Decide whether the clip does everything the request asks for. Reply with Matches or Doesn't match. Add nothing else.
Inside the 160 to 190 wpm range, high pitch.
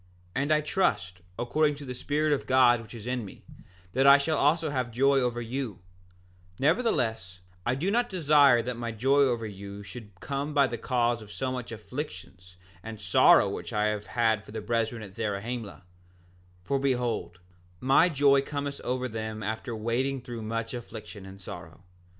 Doesn't match